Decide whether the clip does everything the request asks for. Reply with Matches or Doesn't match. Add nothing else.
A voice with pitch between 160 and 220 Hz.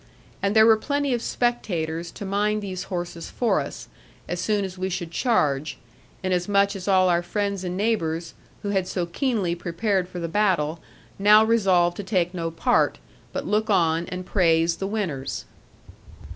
Matches